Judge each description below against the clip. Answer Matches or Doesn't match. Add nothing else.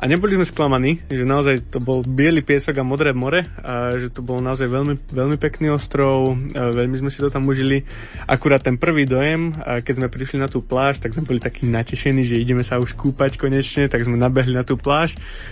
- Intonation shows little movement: Matches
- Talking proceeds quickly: Matches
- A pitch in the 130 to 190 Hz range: Matches